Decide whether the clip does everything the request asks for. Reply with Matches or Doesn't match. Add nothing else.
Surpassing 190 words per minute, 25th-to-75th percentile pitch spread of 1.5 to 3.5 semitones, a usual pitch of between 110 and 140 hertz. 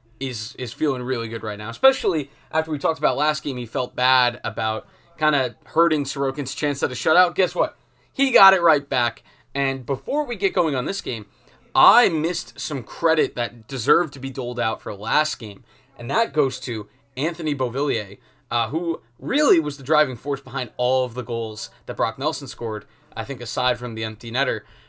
Doesn't match